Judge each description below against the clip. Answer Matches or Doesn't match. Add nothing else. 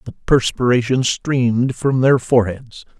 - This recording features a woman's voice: Doesn't match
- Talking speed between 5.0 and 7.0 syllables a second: Doesn't match